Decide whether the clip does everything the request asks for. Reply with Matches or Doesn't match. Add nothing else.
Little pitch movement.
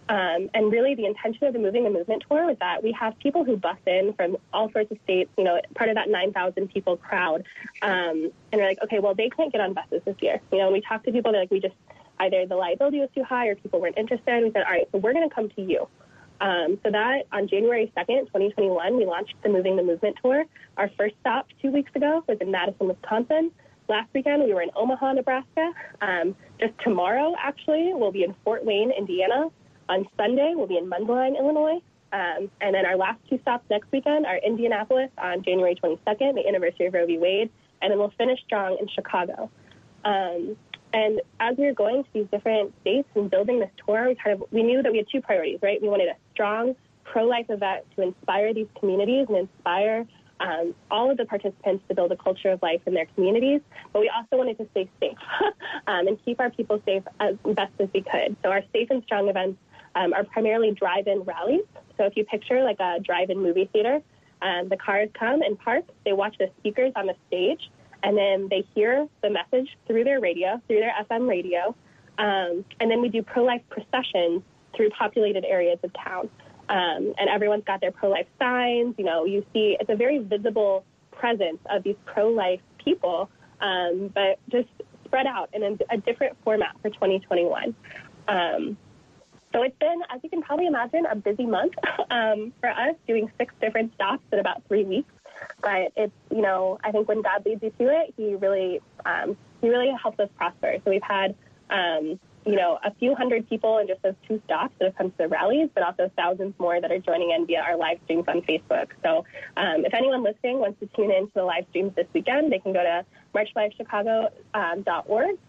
Doesn't match